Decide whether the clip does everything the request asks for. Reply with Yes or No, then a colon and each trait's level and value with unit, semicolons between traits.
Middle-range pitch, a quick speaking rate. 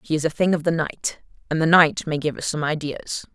Yes: medium, 160 Hz; fast, 270 wpm